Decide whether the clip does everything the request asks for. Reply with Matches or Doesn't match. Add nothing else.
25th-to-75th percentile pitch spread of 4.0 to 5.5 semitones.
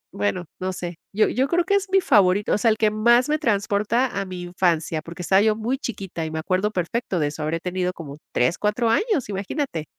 Matches